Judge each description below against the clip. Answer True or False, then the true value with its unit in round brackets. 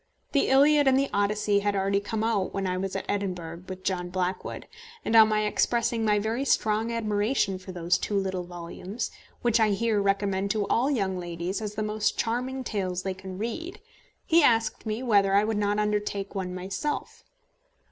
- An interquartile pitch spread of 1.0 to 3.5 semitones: True (3.0 semitones)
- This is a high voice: True (205 Hz)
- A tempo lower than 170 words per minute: False (190 wpm)